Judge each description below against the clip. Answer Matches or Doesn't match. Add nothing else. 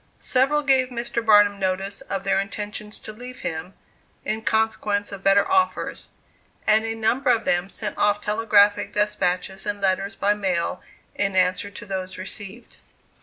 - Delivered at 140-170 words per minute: Matches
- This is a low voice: Doesn't match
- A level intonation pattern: Matches